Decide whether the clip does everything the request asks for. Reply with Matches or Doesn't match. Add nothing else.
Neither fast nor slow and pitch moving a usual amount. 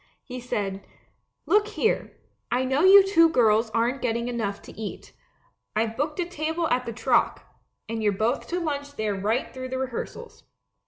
Doesn't match